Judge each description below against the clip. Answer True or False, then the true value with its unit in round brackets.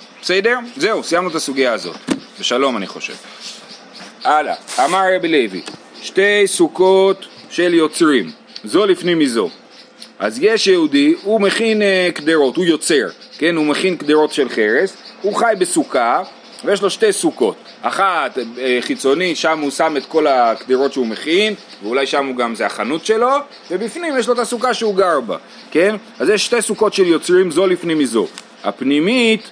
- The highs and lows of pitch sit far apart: True (7.3 semitones)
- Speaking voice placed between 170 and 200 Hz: True (190 Hz)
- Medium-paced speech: False (160 wpm)